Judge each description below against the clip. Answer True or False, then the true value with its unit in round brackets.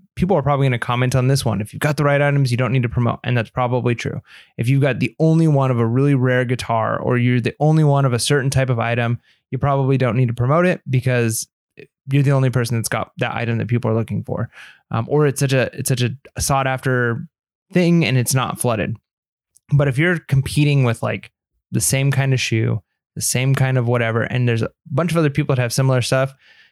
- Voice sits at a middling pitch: False (130 Hz)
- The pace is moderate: False (245 wpm)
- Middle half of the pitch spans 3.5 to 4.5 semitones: False (2.9 semitones)